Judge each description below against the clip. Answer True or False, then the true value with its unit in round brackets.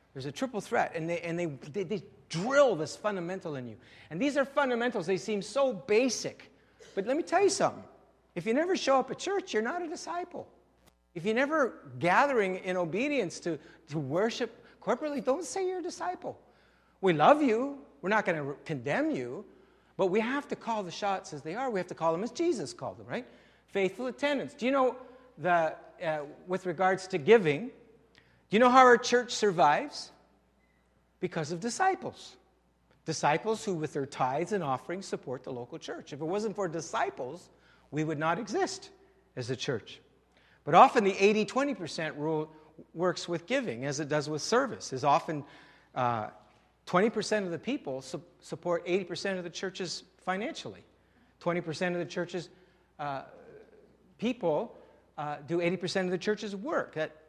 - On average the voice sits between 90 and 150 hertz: False (190 Hz)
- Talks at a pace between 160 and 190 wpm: True (175 wpm)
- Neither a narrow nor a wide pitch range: False (7.0 semitones)